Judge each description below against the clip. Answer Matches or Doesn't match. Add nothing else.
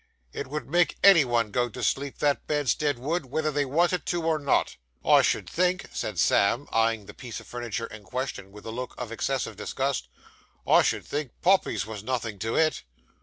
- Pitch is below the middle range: Matches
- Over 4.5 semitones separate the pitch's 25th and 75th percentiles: Matches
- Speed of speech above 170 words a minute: Matches